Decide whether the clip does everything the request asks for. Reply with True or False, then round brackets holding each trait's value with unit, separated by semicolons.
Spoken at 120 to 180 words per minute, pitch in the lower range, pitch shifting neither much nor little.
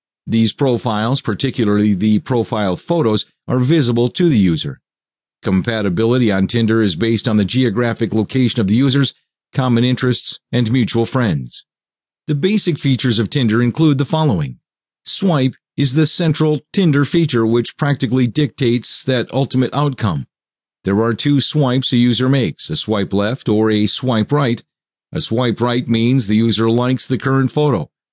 True (155 wpm; 125 Hz; 3.8 semitones)